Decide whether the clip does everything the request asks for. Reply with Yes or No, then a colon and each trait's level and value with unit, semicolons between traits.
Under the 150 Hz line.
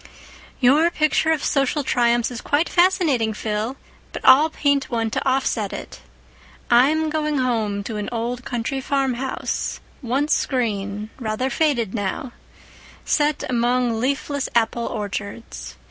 No: very high, 250 Hz